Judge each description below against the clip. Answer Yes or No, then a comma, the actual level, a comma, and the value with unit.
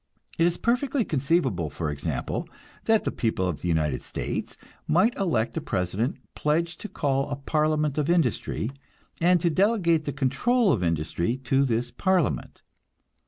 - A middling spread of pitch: No, wide, 7.8 semitones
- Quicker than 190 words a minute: No, average, 155 wpm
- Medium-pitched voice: Yes, medium, 145 Hz